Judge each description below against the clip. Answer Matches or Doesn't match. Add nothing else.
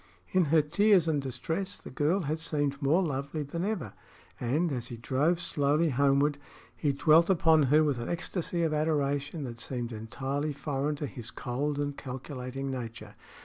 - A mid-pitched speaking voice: Matches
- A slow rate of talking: Doesn't match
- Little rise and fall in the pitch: Doesn't match